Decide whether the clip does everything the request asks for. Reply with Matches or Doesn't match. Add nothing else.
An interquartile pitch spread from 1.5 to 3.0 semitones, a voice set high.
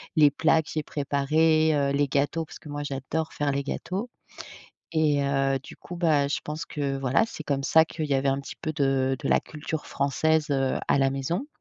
Doesn't match